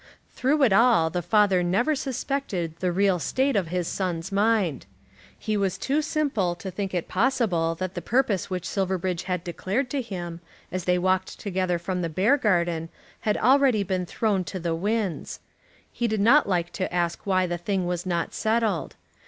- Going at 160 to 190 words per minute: Yes, average, 175 wpm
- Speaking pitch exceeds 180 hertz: Yes, high, 190 Hz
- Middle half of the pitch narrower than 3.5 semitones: No, average, 4.0 semitones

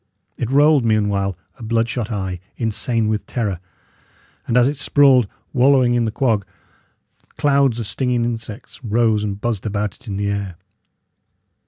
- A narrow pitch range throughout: No, average, 3.2 semitones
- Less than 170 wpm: Yes, average, 155 wpm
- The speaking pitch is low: Yes, low, 115 Hz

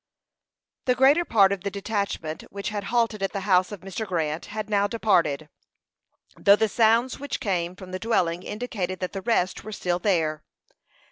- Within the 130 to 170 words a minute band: No, average, 180 wpm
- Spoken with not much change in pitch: No, average, 3.4 semitones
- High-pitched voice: Yes, high, 200 Hz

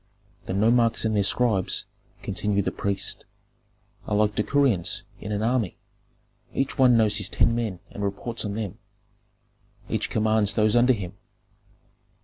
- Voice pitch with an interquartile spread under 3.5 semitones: Yes, narrow, 2.5 semitones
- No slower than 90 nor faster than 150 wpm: Yes, average, 140 wpm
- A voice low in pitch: Yes, low, 105 Hz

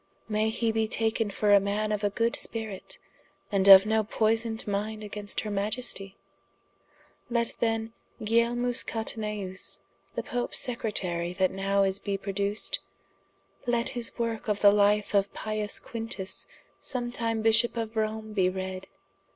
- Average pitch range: No, narrow, 2.2 semitones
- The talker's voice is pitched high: Yes, high, 215 Hz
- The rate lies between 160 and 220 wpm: No, average, 145 wpm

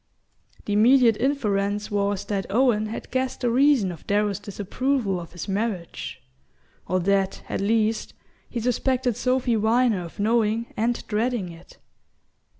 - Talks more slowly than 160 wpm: Yes, average, 140 wpm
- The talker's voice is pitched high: Yes, high, 215 Hz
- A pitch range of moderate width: Yes, average, 3.5 semitones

